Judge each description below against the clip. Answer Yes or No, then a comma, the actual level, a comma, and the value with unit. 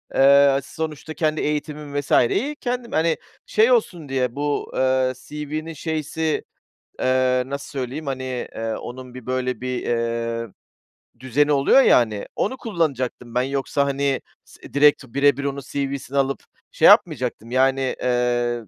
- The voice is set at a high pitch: No, medium, 140 Hz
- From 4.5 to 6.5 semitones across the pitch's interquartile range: No, average, 2.8 semitones